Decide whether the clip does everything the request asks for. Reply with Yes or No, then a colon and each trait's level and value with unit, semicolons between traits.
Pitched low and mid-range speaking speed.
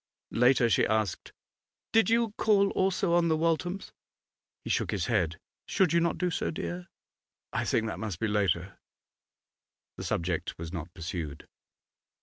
Yes: low, 130 Hz; average, 150 wpm